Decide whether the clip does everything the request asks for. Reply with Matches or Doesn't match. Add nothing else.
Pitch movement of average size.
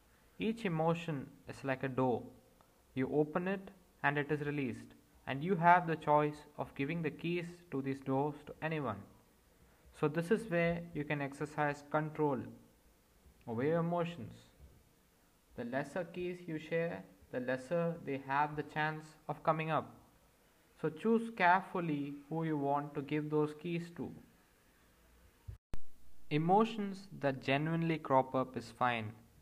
Matches